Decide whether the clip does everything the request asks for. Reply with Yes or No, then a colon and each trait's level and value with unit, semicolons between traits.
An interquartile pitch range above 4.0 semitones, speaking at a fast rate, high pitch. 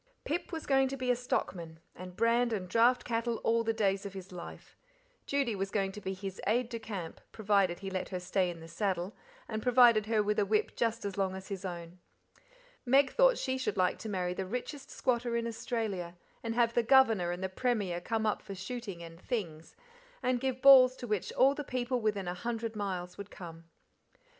Yes: average, 4.5 semitones; fast, 210 wpm; high, 215 Hz